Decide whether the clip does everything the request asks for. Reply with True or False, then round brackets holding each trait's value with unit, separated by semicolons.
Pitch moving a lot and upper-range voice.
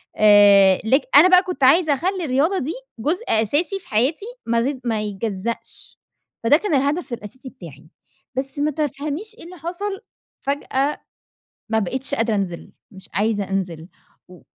True (7.0 semitones; 265 Hz)